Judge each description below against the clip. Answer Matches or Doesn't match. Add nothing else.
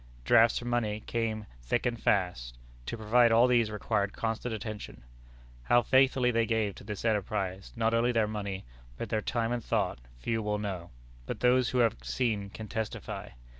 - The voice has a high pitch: Doesn't match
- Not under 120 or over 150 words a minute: Doesn't match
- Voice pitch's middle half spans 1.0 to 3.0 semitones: Matches